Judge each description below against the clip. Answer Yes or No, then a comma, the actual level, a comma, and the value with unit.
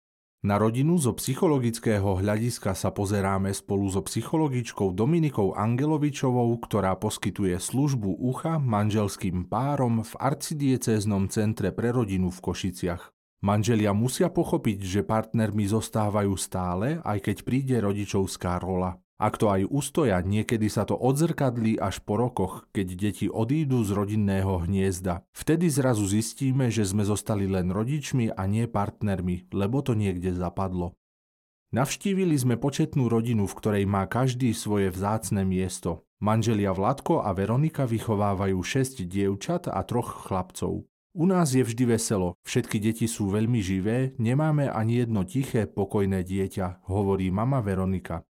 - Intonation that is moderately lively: Yes, average, 4.4 semitones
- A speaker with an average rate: Yes, average, 135 wpm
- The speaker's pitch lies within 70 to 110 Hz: Yes, low, 105 Hz